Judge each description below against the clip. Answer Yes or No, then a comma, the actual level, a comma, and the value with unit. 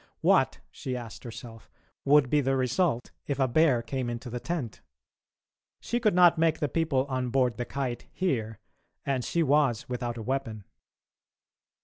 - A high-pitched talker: No, low, 130 Hz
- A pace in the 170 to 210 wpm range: No, average, 160 wpm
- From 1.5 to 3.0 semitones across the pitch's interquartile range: No, average, 3.7 semitones